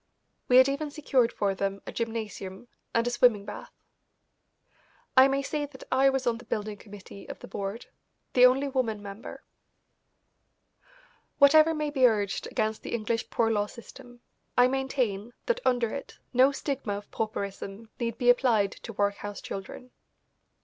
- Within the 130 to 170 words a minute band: Yes, average, 155 wpm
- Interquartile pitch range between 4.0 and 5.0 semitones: Yes, average, 4.4 semitones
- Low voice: No, high, 235 Hz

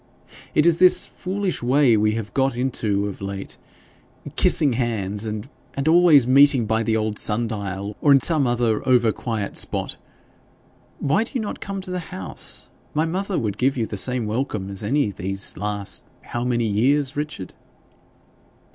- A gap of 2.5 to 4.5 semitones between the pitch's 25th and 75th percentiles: No, wide, 5.5 semitones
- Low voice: Yes, low, 120 Hz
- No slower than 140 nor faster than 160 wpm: No, average, 175 wpm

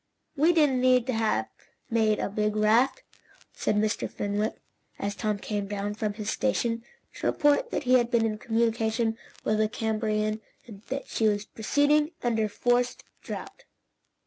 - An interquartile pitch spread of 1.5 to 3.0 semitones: Yes, average, 2.7 semitones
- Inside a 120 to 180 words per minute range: Yes, average, 160 wpm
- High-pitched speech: Yes, high, 225 Hz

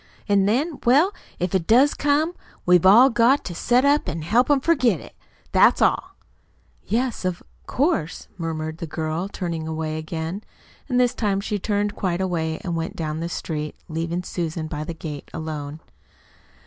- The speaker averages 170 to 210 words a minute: Yes, average, 175 wpm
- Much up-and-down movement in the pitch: Yes, wide, 6.9 semitones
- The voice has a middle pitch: Yes, medium, 180 Hz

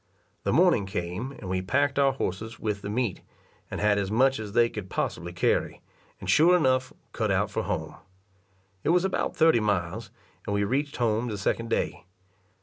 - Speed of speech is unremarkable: Yes, average, 185 wpm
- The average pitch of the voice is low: Yes, low, 110 Hz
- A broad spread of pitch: No, average, 4.7 semitones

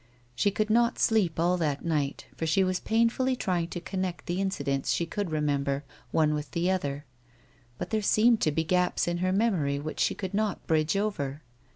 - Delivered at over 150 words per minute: Yes, average, 195 wpm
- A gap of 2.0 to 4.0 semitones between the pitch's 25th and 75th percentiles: No, average, 4.9 semitones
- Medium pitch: Yes, medium, 175 Hz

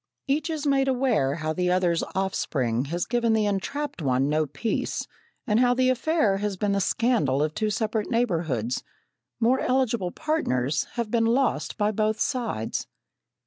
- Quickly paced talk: No, average, 160 wpm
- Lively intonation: Yes, wide, 7.5 semitones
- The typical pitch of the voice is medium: No, high, 210 Hz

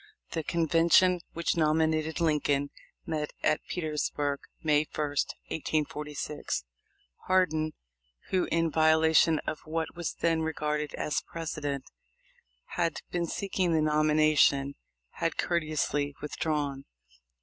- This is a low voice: No, medium, 155 Hz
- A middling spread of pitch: No, narrow, 1.7 semitones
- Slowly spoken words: Yes, slow, 105 wpm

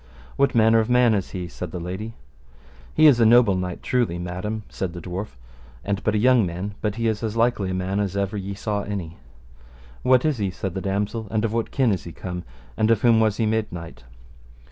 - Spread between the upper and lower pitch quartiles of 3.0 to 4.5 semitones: Yes, average, 3.5 semitones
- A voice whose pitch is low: Yes, low, 105 Hz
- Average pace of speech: No, fast, 230 wpm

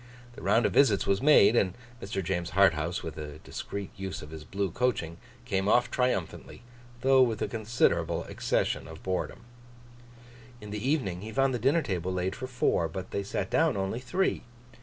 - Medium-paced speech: Yes, average, 180 wpm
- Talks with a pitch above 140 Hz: No, low, 100 Hz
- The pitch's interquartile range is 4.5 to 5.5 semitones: Yes, average, 5.2 semitones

